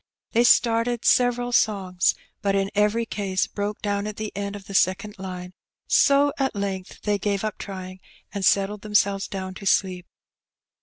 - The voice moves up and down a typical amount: No, narrow, 2.0 semitones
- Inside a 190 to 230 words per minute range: No, average, 165 wpm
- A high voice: Yes, high, 200 Hz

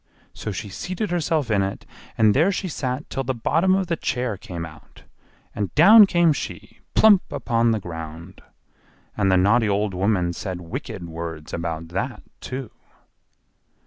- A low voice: Yes, low, 110 Hz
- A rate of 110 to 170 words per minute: Yes, average, 160 wpm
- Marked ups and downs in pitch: Yes, wide, 9.0 semitones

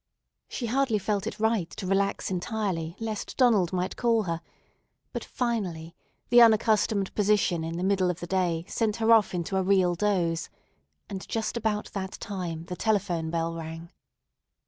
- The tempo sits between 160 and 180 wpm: Yes, average, 165 wpm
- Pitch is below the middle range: No, high, 195 Hz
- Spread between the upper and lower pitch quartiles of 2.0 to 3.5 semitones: No, average, 4.2 semitones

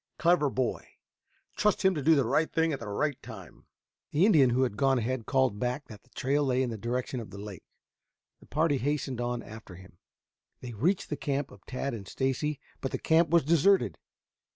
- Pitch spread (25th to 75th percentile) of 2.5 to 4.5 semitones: Yes, average, 3.9 semitones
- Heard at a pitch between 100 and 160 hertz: Yes, low, 135 Hz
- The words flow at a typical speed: No, fast, 210 wpm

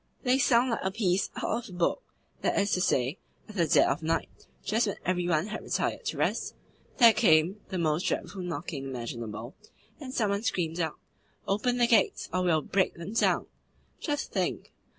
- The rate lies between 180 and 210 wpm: Yes, average, 190 wpm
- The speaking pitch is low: No, medium, 185 Hz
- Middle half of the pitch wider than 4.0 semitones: Yes, wide, 5.5 semitones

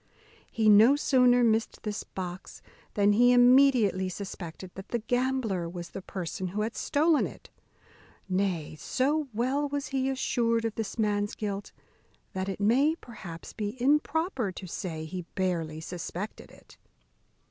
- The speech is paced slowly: No, average, 145 wpm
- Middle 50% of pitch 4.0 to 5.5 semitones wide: Yes, average, 5.2 semitones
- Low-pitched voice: No, high, 215 Hz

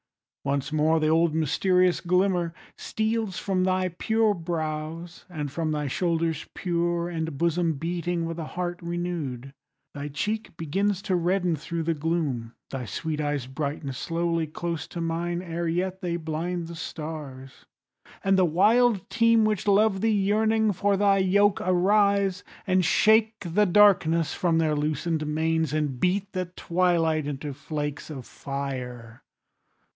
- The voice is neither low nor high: Yes, medium, 170 Hz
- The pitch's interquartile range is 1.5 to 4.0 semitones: Yes, average, 3.4 semitones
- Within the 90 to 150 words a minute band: Yes, average, 145 wpm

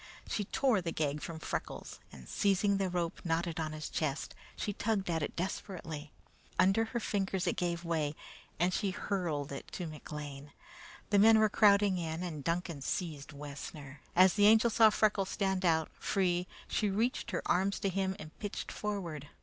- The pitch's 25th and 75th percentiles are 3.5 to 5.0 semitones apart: Yes, average, 4.3 semitones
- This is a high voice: No, medium, 180 Hz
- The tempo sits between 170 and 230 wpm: Yes, average, 175 wpm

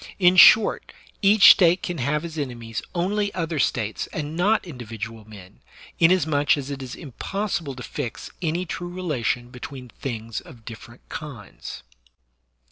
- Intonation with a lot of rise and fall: Yes, wide, 6.7 semitones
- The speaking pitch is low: No, medium, 145 Hz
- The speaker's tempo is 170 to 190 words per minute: No, average, 140 wpm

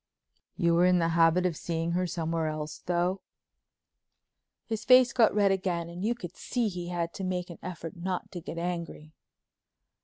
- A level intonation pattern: Yes, narrow, 1.8 semitones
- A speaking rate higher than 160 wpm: Yes, average, 180 wpm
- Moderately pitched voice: Yes, medium, 175 Hz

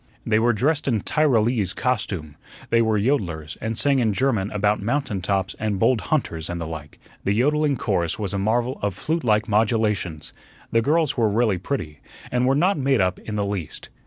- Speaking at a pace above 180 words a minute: Yes, average, 190 wpm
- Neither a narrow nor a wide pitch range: Yes, average, 4.7 semitones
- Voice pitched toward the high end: No, low, 110 Hz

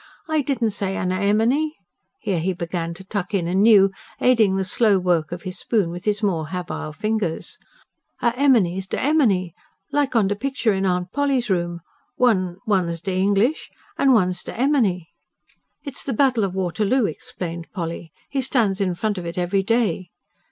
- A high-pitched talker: Yes, high, 195 Hz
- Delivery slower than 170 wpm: No, average, 175 wpm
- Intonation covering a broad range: No, average, 4.6 semitones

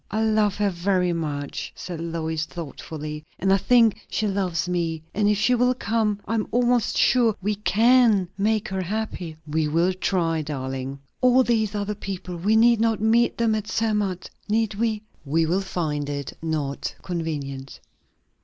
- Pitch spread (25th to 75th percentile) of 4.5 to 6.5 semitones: Yes, average, 5.2 semitones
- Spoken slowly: No, average, 165 wpm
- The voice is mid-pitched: No, high, 195 Hz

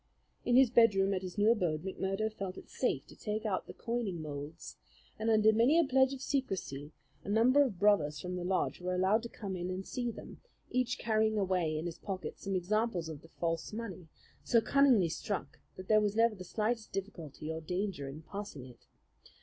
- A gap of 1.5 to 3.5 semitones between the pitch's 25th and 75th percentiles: No, average, 4.4 semitones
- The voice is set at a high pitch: Yes, high, 195 Hz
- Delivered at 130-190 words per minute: No, fast, 205 wpm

